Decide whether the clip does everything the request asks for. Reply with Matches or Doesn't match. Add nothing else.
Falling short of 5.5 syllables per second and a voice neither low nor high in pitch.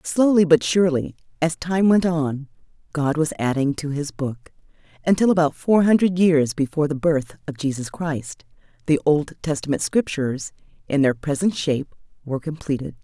Matches